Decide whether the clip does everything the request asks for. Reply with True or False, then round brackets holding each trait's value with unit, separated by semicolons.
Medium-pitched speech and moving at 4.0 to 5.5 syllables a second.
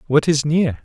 True (145 Hz; 4.7 syllables/s)